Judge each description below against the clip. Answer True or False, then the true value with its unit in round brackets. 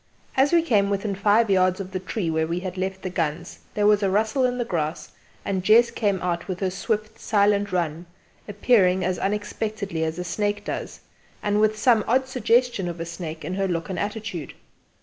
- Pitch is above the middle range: True (200 Hz)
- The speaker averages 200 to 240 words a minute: True (205 wpm)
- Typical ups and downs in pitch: True (3.1 semitones)